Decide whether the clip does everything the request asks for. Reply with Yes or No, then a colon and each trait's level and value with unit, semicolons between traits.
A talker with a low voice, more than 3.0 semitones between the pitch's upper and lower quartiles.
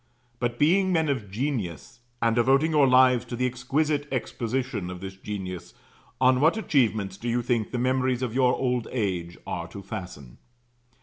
Yes: low, 120 Hz; average, 4.5 semitones